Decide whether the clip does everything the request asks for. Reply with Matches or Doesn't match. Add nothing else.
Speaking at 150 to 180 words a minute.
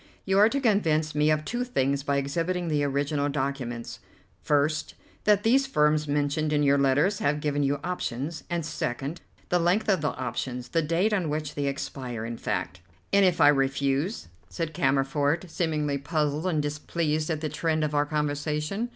Matches